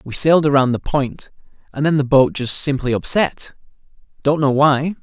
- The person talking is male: Yes, male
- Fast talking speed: No, average, 165 wpm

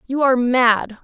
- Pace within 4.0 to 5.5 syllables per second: Yes, 4.8 syllables/s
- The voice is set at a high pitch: Yes, very high, 250 Hz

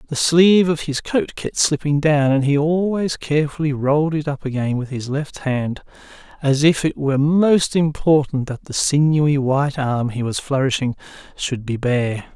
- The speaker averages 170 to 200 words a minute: Yes, average, 180 wpm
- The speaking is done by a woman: No, male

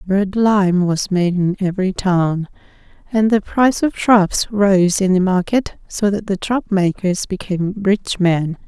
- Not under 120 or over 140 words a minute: No, average, 165 wpm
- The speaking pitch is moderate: No, high, 195 Hz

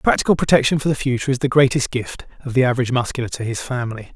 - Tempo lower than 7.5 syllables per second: No, 7.7 syllables/s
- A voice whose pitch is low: Yes, low, 130 Hz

